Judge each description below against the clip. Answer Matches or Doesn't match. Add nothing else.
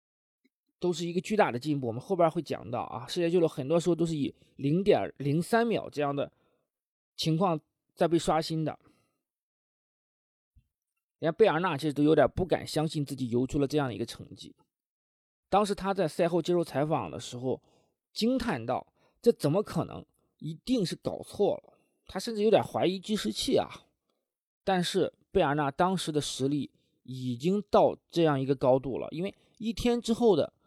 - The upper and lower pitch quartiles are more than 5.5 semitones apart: Doesn't match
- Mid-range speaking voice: Matches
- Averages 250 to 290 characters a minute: Matches